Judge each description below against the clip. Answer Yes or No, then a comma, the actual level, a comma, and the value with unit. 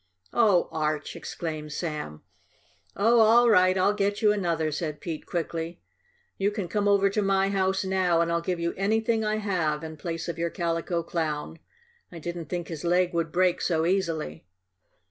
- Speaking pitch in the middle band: Yes, medium, 175 Hz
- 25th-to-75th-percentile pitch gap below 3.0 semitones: No, average, 3.3 semitones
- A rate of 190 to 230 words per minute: No, average, 175 wpm